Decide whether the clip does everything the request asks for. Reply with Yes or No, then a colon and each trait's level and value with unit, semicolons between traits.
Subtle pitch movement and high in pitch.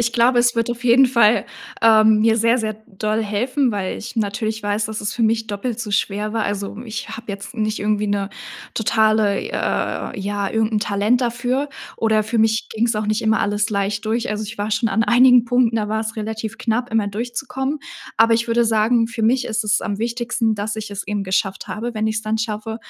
Yes: narrow, 1.8 semitones; high, 220 Hz